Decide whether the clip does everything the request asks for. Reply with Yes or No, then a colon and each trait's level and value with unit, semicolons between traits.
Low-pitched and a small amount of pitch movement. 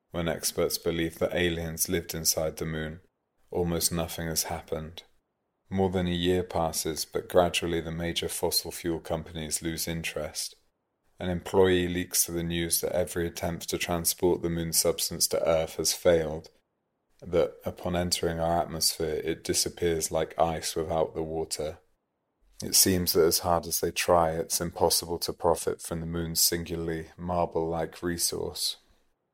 Yes: very low, 85 Hz; narrow, 1.2 semitones